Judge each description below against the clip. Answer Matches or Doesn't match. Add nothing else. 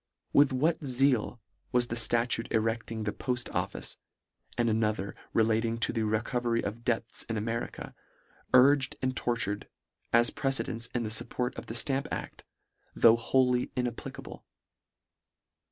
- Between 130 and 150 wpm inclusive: Matches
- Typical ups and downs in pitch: Doesn't match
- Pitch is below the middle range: Matches